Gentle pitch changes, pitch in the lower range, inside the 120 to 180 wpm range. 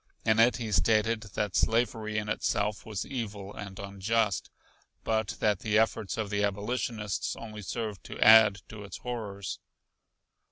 Yes: narrow, 1.7 semitones; low, 105 Hz; average, 150 wpm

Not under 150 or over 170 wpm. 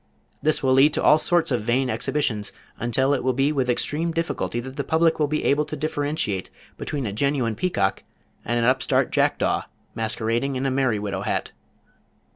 No: average, 190 wpm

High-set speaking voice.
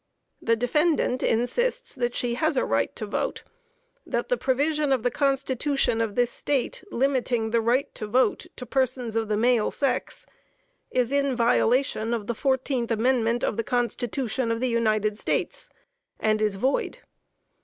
Yes: high, 245 Hz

